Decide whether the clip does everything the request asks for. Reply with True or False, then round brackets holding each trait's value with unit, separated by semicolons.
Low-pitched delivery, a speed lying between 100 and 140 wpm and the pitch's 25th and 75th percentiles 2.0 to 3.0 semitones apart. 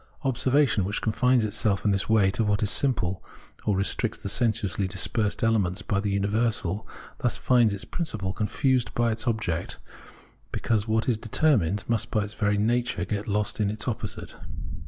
False (110 Hz; 170 wpm; 2.6 semitones)